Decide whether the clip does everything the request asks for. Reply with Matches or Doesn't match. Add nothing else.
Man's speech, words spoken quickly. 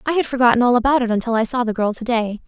Doesn't match